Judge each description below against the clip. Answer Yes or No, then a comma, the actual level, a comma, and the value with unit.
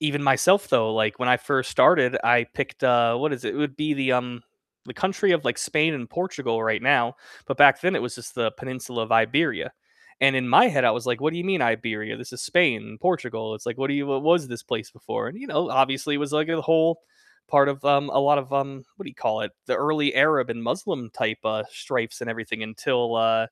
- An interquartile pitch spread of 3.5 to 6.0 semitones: Yes, average, 4.1 semitones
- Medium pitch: No, low, 130 Hz